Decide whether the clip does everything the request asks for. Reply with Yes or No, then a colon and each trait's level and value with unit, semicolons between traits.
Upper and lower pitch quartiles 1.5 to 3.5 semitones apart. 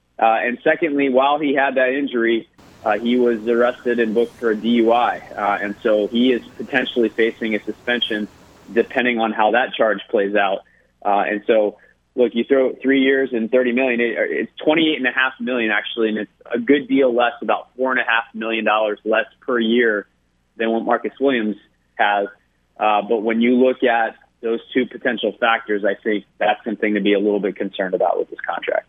Yes: average, 2.9 semitones